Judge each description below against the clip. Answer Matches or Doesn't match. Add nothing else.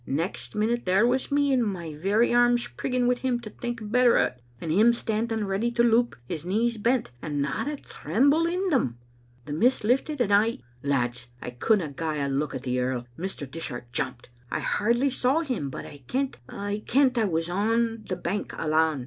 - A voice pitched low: Doesn't match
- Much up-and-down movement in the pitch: Matches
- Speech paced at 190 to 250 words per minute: Matches